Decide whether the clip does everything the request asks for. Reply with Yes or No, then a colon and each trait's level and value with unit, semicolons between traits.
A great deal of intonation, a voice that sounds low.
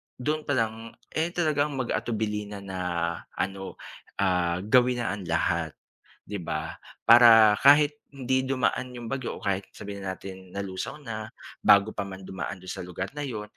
No: average, 4.9 semitones; low, 105 Hz